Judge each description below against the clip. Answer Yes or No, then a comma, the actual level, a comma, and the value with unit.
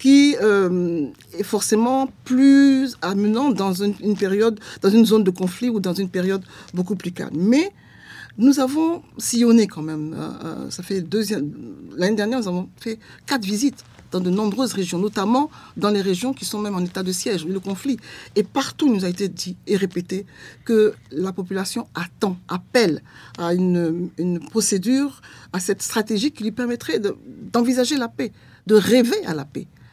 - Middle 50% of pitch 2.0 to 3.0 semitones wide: No, average, 4.5 semitones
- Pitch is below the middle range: No, high, 205 Hz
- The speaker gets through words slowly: No, average, 175 wpm